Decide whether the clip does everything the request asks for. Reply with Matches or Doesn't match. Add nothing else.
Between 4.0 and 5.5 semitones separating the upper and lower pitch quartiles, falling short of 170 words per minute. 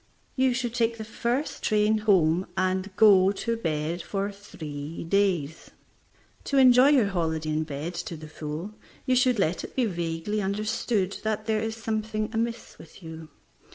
Matches